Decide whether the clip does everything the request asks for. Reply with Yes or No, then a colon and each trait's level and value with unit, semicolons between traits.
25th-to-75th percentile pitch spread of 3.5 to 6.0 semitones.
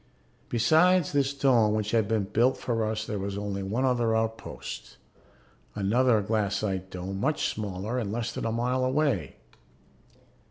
Yes: average, 3.8 semitones